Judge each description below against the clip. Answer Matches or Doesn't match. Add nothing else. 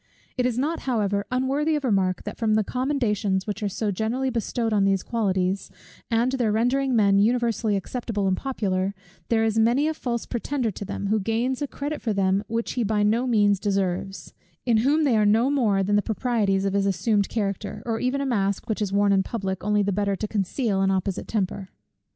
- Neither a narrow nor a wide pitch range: Matches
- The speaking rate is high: Matches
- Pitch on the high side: Matches